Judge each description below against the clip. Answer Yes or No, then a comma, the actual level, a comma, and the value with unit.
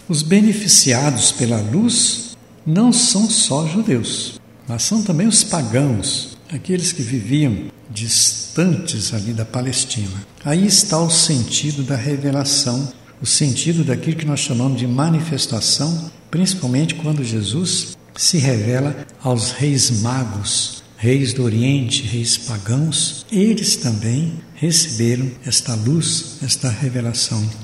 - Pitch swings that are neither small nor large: Yes, average, 5.0 semitones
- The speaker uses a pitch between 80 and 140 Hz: Yes, low, 135 Hz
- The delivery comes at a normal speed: No, slow, 115 wpm